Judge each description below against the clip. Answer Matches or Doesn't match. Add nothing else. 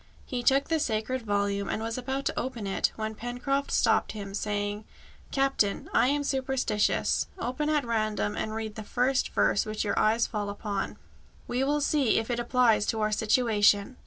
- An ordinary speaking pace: Matches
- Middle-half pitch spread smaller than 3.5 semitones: Doesn't match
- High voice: Matches